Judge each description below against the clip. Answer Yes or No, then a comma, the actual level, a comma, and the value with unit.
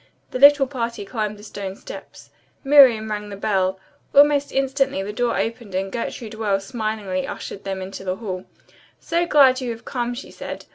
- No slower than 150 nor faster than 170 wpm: No, average, 180 wpm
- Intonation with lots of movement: No, average, 5.0 semitones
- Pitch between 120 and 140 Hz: No, high, 220 Hz